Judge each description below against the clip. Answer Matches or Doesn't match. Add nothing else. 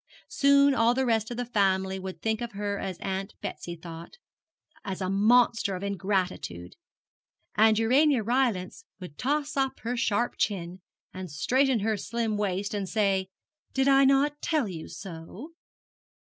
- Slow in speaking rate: Doesn't match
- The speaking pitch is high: Matches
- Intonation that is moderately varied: Matches